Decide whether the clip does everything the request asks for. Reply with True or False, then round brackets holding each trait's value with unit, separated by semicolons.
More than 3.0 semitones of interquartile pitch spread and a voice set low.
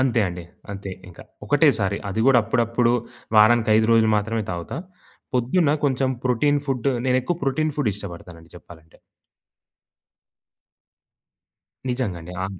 True (5.1 semitones; 115 Hz)